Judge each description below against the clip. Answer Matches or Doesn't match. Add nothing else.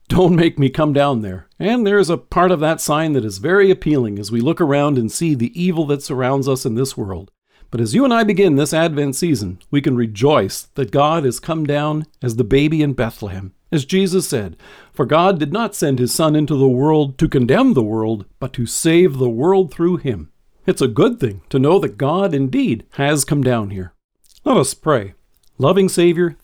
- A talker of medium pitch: Matches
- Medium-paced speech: Doesn't match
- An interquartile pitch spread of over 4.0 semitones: Matches